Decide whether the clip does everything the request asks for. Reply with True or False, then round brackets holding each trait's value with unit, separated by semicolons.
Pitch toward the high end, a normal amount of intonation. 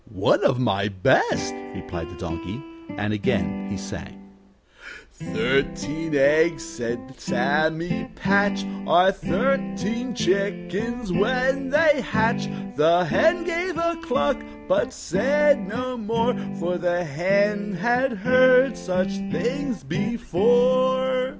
False (195 Hz; 7.8 semitones)